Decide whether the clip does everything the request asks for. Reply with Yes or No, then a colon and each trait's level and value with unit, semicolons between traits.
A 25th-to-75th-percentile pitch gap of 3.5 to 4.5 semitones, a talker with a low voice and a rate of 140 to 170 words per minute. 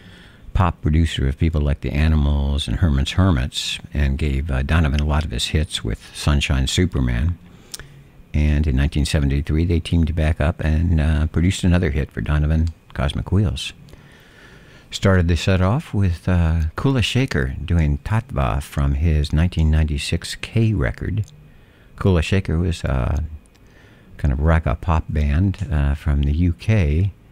Yes: average, 4.1 semitones; very low, 80 Hz; average, 145 wpm